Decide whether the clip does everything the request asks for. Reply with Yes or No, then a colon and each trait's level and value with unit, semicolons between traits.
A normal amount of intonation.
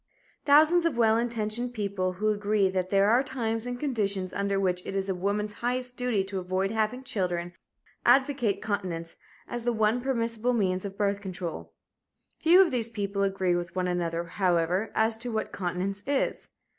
Yes: average, 4.3 semitones